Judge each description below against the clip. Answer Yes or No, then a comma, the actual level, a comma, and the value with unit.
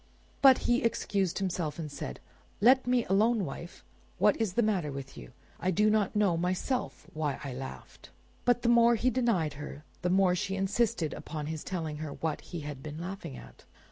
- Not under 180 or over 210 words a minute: Yes, average, 190 wpm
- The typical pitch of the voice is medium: Yes, medium, 180 Hz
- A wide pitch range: Yes, wide, 6.3 semitones